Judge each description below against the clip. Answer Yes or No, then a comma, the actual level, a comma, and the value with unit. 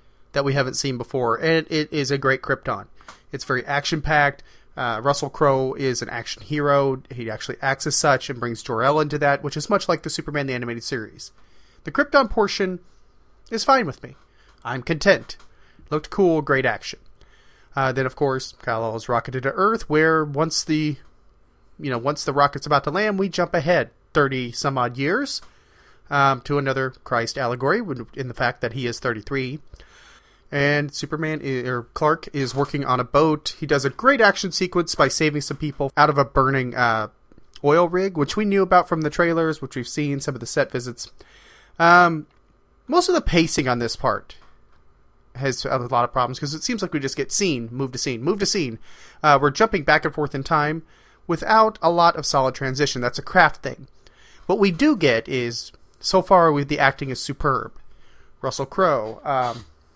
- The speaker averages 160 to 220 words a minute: Yes, average, 195 wpm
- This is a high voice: No, medium, 140 Hz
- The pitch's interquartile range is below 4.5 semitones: Yes, average, 3.8 semitones